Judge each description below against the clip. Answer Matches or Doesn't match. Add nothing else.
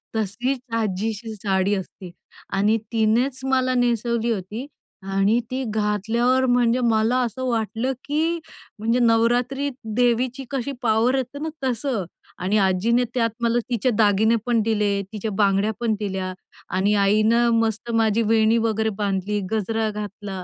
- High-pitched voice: Matches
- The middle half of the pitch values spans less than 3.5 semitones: Matches